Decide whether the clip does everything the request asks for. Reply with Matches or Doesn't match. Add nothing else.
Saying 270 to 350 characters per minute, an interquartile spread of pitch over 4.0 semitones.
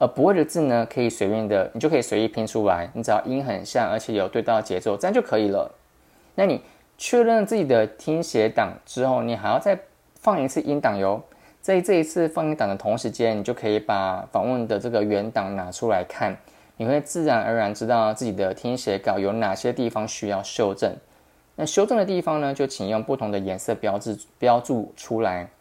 Matches